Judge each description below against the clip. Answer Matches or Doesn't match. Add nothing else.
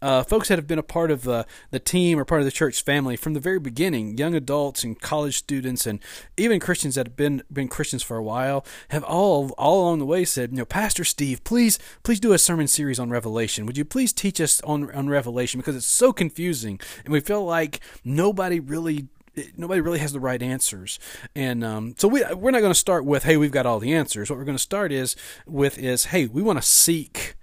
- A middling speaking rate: Doesn't match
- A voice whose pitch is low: Doesn't match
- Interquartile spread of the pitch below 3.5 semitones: Doesn't match